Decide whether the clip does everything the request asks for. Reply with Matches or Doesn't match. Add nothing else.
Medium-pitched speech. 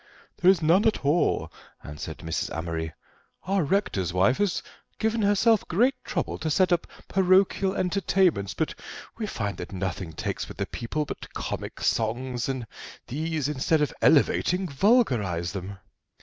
Matches